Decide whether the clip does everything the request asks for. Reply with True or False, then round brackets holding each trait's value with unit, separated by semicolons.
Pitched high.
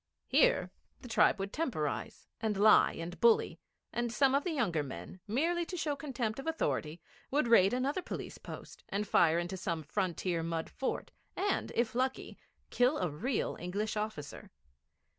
True (220 Hz)